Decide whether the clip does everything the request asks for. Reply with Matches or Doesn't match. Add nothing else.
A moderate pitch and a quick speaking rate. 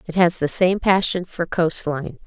Matches